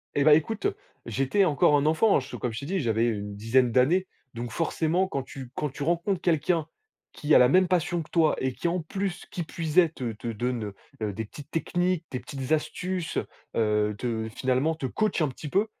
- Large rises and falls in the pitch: Yes, wide, 5.8 semitones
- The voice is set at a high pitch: No, medium, 150 Hz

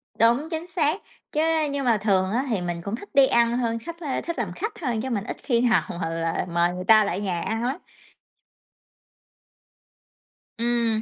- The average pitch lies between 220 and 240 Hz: Yes, high, 230 Hz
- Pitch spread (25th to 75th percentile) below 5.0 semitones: No, wide, 5.6 semitones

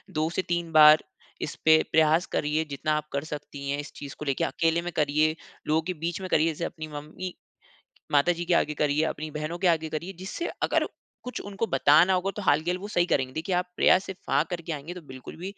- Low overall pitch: No, medium, 160 Hz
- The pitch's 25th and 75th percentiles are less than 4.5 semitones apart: Yes, average, 2.7 semitones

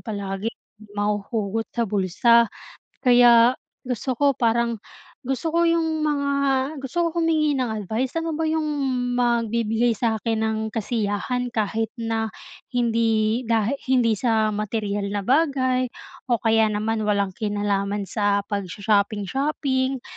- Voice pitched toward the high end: Yes, high, 230 Hz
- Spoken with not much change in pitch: No, average, 3.5 semitones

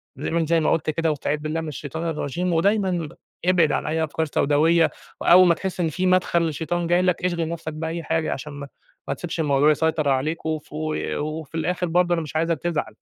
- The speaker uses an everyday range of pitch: No, narrow, 2.0 semitones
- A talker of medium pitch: Yes, medium, 160 Hz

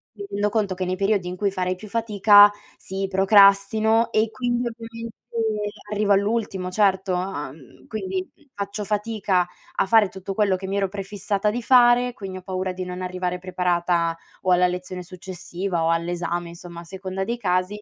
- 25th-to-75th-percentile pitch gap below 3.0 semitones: Yes, narrow, 2.5 semitones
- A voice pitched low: No, high, 195 Hz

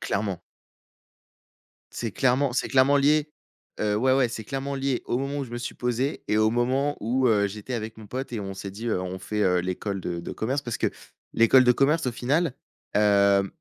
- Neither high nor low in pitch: No, low, 120 Hz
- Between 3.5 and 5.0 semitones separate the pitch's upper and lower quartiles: Yes, average, 4.5 semitones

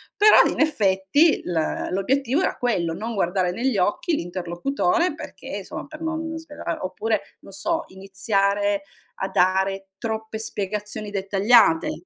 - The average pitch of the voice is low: No, high, 205 Hz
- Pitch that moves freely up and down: Yes, wide, 5.8 semitones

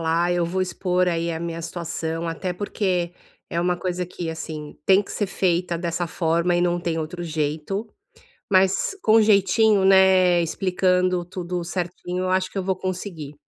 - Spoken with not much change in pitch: Yes, narrow, 1.9 semitones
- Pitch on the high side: No, medium, 180 Hz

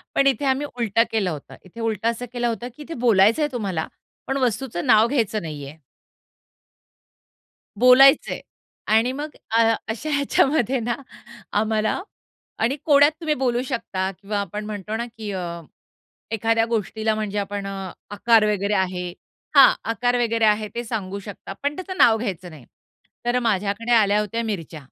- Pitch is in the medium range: No, high, 225 Hz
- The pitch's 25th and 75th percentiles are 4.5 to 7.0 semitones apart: No, average, 3.4 semitones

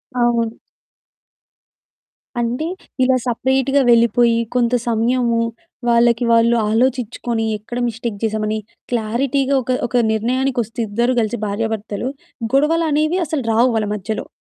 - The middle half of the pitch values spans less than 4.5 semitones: Yes, narrow, 2.4 semitones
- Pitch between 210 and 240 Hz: Yes, high, 235 Hz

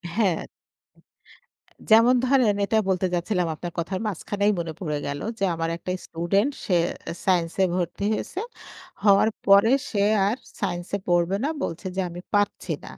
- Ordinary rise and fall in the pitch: Yes, average, 3.1 semitones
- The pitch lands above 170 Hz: Yes, high, 190 Hz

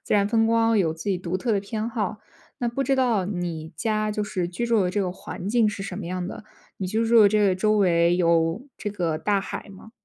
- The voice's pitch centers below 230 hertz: Yes, high, 205 Hz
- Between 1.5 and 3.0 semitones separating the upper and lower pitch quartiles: No, average, 3.7 semitones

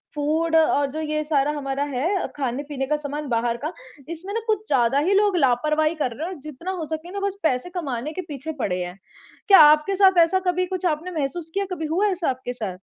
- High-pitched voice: Yes, very high, 310 Hz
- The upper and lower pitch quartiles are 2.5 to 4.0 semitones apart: No, average, 4.7 semitones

